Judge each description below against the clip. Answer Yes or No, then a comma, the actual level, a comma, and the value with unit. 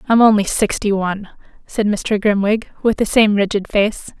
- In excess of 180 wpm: No, average, 170 wpm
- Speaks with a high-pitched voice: Yes, high, 210 Hz